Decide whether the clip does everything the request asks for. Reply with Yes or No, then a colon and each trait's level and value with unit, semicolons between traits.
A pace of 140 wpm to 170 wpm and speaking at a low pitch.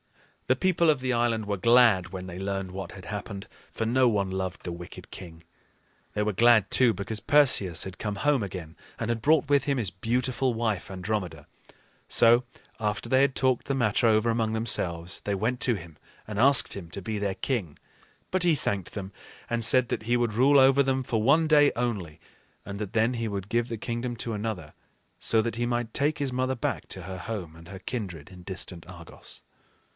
No: fast, 205 wpm; low, 110 Hz